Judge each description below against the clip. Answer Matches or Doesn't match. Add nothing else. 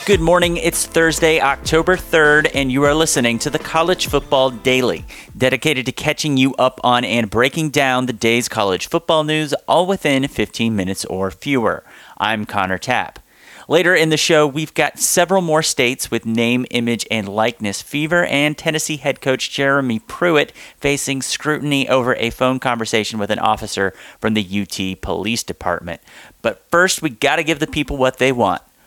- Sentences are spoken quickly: Doesn't match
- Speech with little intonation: Doesn't match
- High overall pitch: Doesn't match